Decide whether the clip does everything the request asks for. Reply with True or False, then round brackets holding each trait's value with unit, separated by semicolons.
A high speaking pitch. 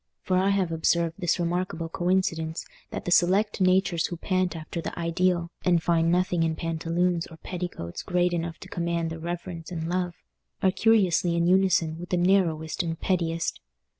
False (175 Hz)